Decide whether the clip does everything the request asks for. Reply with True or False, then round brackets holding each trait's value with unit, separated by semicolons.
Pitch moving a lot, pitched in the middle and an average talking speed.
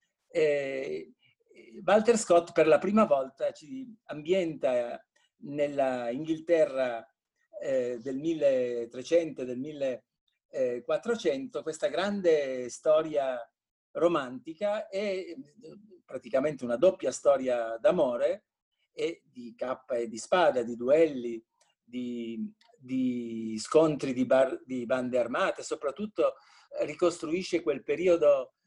False (8.5 semitones; 155 Hz; 90 wpm)